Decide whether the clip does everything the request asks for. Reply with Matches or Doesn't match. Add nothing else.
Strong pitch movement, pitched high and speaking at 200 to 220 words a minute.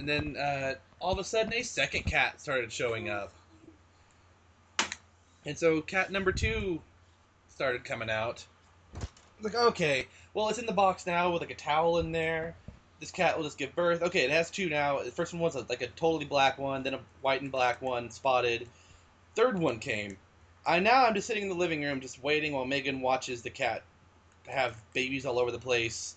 Doesn't match